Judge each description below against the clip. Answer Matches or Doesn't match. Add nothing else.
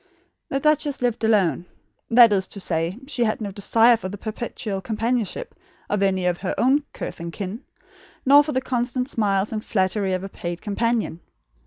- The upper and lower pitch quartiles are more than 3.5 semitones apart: Matches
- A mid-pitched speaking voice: Doesn't match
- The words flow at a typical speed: Matches